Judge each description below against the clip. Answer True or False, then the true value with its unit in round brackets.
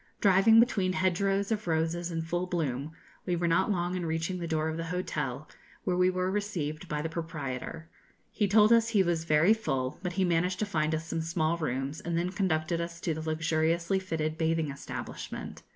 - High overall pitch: False (170 Hz)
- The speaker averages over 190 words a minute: True (200 wpm)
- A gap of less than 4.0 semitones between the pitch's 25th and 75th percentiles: True (2.7 semitones)